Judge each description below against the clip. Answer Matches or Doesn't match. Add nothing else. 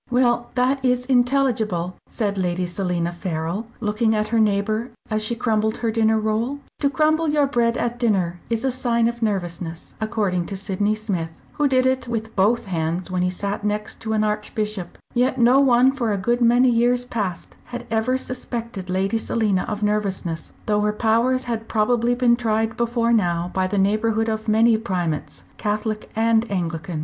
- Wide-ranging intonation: Doesn't match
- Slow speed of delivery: Doesn't match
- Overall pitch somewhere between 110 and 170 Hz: Doesn't match